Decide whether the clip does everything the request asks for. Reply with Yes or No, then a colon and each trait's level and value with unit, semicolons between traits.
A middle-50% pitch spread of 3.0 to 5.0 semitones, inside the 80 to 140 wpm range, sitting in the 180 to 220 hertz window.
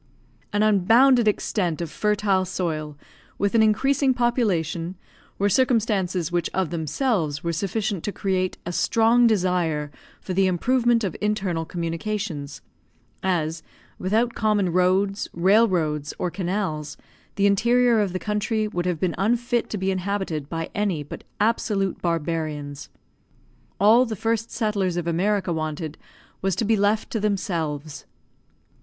Yes: average, 4.2 semitones; slow, 135 wpm; high, 190 Hz